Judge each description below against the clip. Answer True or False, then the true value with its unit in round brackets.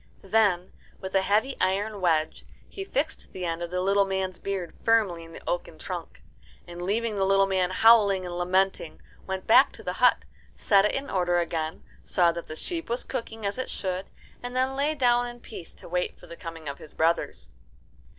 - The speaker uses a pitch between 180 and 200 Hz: True (190 Hz)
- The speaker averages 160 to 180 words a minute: False (200 wpm)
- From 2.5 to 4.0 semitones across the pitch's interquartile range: False (4.4 semitones)